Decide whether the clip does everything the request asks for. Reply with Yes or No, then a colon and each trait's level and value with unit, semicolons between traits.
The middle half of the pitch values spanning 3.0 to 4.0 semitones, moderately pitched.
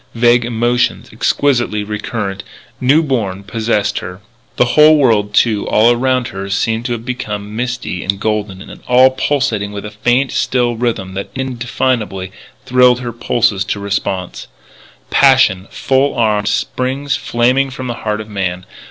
No: average, 3.6 semitones; low, 115 Hz